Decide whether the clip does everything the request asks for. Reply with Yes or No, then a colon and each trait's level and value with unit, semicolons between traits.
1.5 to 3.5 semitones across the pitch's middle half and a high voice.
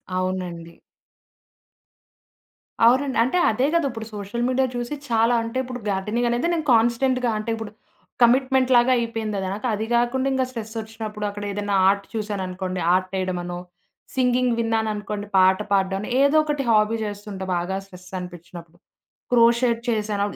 No: average, 3.9 semitones; high, 220 Hz